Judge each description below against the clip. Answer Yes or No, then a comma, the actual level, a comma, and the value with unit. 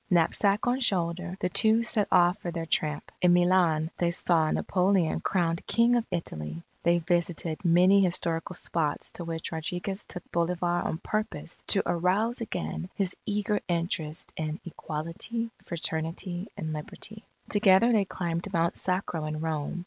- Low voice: No, medium, 175 Hz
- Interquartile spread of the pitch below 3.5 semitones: Yes, average, 3.1 semitones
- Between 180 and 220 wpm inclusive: No, average, 150 wpm